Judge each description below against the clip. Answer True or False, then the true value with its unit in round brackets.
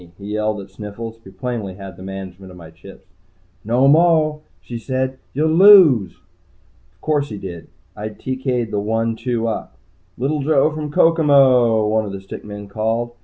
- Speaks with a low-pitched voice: True (115 Hz)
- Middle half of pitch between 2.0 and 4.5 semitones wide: False (5.2 semitones)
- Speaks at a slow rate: False (170 wpm)